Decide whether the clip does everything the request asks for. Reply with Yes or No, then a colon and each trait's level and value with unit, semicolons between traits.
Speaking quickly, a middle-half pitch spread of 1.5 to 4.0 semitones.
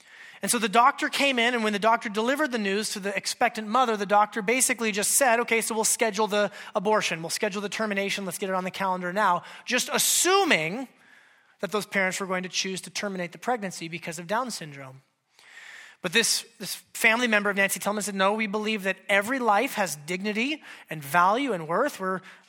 Yes: fast, 210 wpm; average, 3.6 semitones